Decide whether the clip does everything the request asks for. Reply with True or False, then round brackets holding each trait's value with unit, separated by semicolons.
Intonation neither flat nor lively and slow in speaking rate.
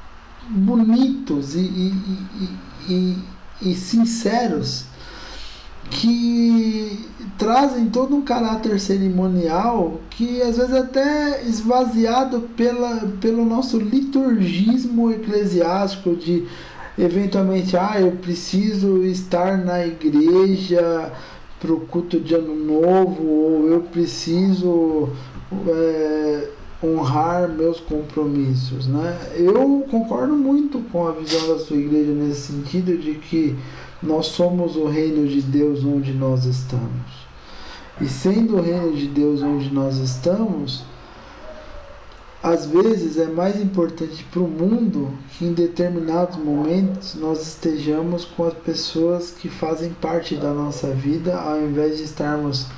True (5.0 semitones; 115 wpm)